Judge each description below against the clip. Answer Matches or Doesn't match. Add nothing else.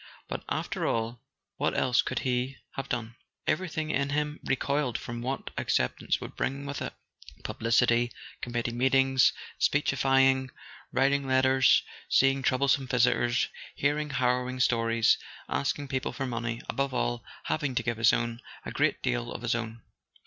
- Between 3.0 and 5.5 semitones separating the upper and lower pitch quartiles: Doesn't match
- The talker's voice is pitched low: Matches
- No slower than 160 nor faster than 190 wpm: Doesn't match